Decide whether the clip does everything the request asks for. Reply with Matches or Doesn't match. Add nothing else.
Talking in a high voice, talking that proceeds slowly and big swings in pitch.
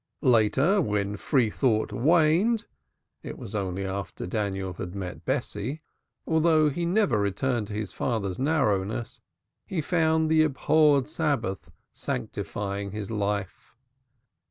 Doesn't match